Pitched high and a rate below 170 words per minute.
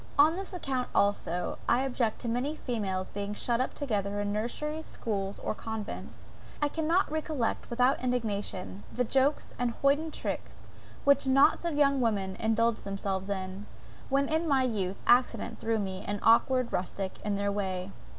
Yes: high, 230 Hz; average, 160 wpm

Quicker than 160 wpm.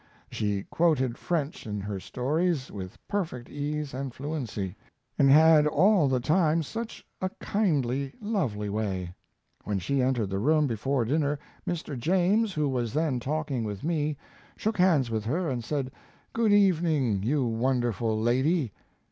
No: average, 150 wpm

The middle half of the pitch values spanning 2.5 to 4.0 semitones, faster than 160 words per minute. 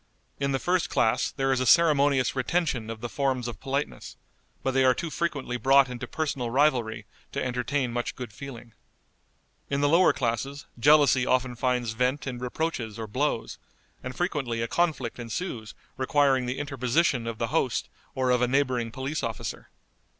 Yes: average, 2.8 semitones; average, 170 wpm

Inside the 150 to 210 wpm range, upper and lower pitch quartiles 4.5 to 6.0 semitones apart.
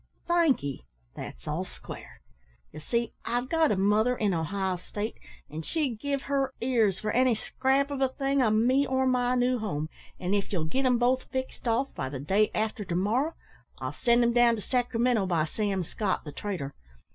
Yes: average, 190 wpm; average, 5.2 semitones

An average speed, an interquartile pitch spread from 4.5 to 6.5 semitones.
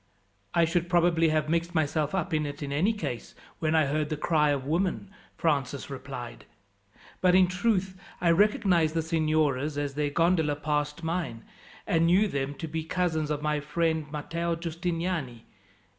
No: average, 165 wpm; average, 2.7 semitones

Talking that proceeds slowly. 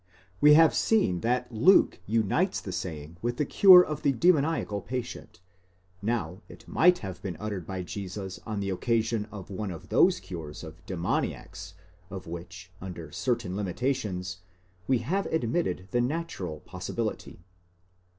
No: average, 150 wpm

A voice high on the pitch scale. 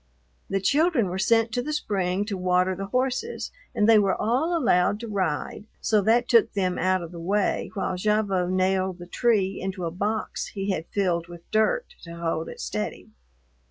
Yes: high, 195 Hz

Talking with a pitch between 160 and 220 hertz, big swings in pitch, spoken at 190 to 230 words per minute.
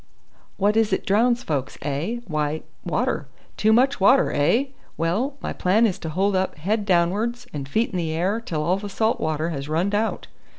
Yes: high, 190 Hz; wide, 5.9 semitones; average, 195 wpm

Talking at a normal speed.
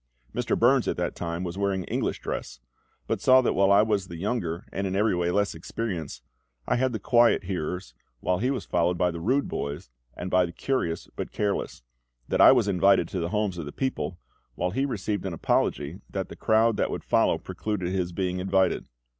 No: fast, 210 wpm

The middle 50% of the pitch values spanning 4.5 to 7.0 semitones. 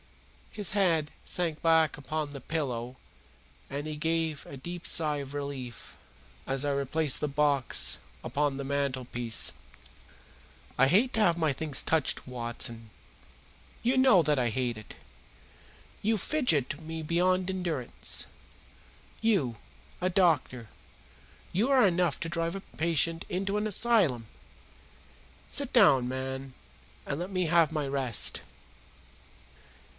Yes: average, 4.8 semitones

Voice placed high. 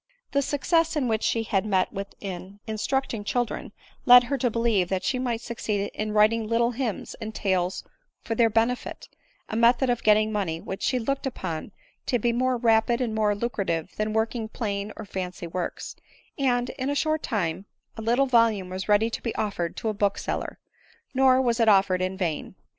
Yes: high, 220 Hz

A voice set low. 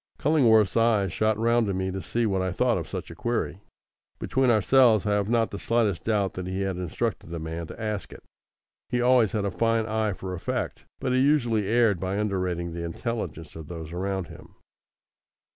Yes: low, 105 Hz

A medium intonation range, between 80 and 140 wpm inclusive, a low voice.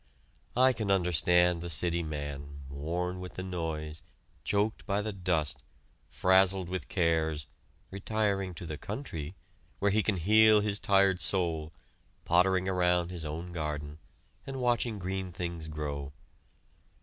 Yes: average, 3.6 semitones; slow, 135 wpm; very low, 90 Hz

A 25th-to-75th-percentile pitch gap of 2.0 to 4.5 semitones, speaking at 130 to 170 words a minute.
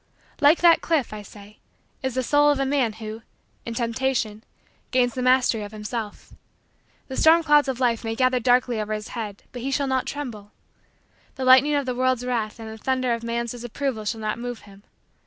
No: average, 3.1 semitones; average, 200 wpm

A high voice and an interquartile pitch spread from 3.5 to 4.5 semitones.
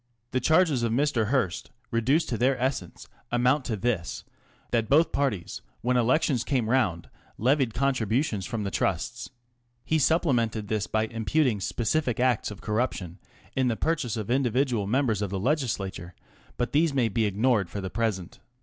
No: low, 120 Hz; average, 4.0 semitones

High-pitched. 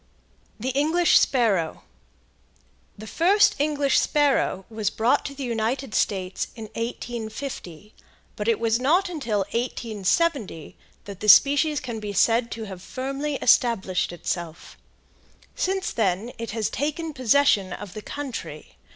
Yes: high, 230 Hz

